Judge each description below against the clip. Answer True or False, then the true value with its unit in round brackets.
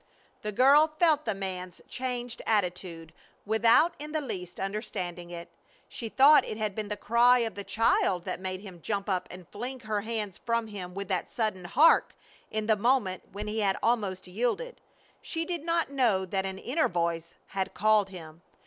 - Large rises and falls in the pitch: False (4.6 semitones)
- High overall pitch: True (210 Hz)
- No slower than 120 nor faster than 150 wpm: False (185 wpm)